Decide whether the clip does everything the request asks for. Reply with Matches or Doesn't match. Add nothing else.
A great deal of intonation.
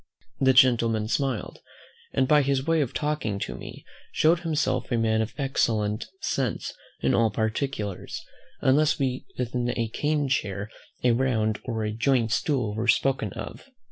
Doesn't match